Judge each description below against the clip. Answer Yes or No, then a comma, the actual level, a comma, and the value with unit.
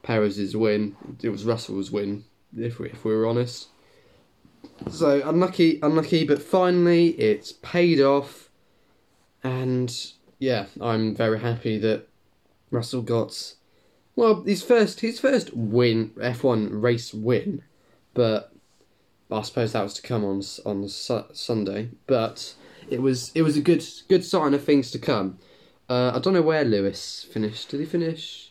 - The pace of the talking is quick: No, average, 150 wpm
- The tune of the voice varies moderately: No, wide, 6.2 semitones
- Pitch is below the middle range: Yes, low, 120 Hz